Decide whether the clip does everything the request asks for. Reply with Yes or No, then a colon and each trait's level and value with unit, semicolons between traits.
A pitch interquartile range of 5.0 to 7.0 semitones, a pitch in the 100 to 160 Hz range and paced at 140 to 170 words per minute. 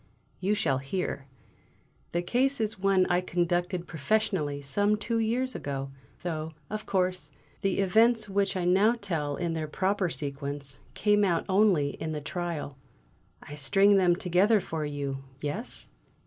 No: wide, 5.4 semitones; medium, 180 Hz; average, 150 wpm